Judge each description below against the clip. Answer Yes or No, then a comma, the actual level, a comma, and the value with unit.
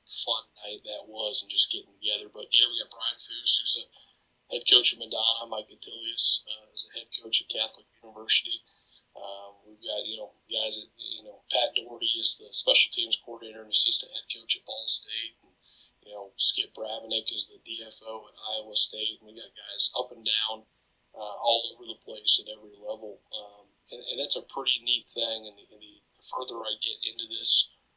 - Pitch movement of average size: No, narrow, 1.6 semitones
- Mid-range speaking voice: No, low, 110 Hz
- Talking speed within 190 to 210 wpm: Yes, fast, 205 wpm